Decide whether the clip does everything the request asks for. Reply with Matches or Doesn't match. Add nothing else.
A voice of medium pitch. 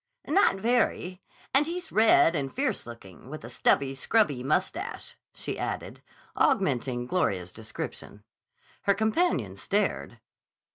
Matches